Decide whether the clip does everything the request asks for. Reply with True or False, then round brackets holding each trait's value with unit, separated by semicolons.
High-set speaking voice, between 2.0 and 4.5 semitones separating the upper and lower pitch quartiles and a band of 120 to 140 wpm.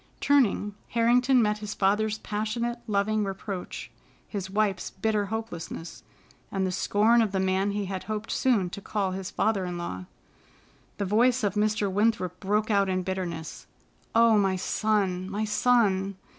False (205 Hz; 2.4 semitones; 155 wpm)